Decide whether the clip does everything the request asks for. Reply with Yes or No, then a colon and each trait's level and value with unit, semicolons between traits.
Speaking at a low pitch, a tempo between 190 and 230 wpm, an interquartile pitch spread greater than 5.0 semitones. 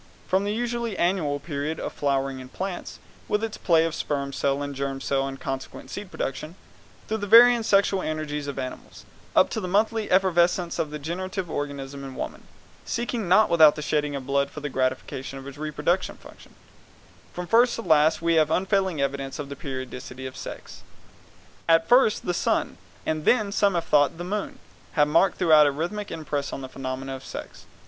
No: medium, 155 Hz; average, 195 wpm; wide, 5.4 semitones